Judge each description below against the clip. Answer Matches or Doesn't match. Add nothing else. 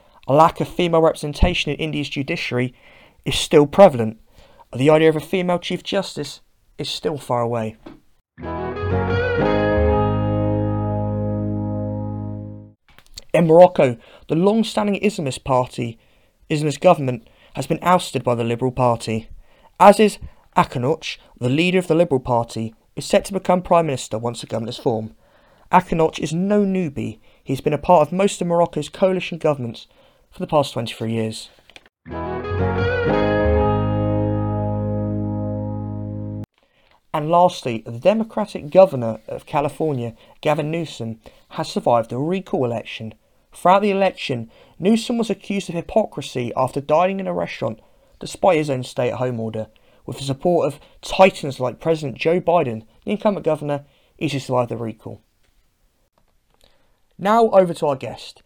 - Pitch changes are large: Matches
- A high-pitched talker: Doesn't match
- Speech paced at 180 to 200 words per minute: Doesn't match